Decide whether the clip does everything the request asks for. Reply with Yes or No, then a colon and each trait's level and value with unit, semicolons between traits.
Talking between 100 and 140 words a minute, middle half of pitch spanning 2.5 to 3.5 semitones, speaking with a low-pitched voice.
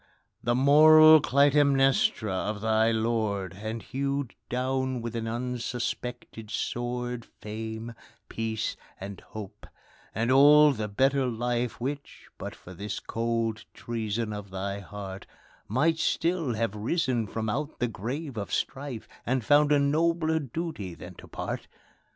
No: slow, 135 wpm; average, 4.2 semitones; low, 120 Hz